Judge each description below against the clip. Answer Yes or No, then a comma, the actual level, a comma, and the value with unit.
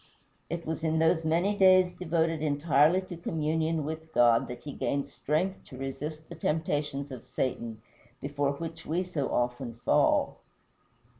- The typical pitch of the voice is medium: Yes, medium, 155 Hz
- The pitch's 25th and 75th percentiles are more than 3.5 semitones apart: No, average, 2.9 semitones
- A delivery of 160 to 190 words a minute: No, average, 150 wpm